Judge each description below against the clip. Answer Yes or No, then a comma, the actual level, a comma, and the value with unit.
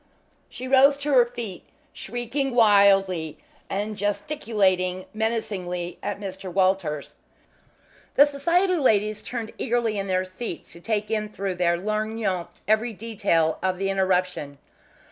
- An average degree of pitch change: Yes, average, 3.9 semitones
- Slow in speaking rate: Yes, slow, 125 wpm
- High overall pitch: Yes, high, 205 Hz